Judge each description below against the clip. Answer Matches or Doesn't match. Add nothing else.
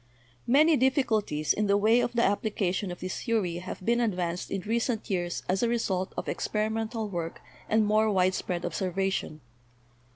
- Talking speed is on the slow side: Doesn't match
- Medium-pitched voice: Doesn't match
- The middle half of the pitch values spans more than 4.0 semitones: Doesn't match